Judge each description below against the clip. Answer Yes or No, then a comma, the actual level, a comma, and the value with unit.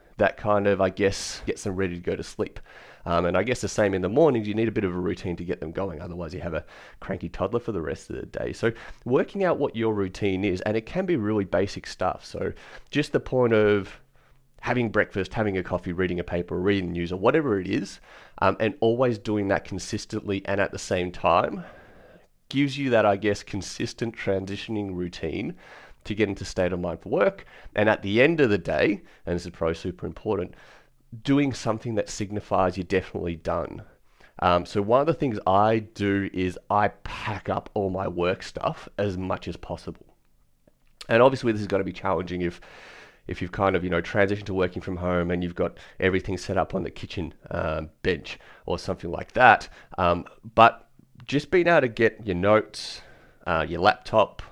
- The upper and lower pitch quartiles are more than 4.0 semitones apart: No, average, 3.5 semitones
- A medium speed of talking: No, fast, 210 wpm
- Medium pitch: No, low, 100 Hz